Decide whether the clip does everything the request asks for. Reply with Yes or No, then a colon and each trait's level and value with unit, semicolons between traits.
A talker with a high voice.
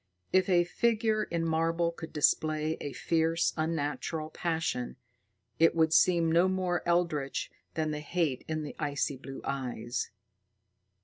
No: medium, 160 Hz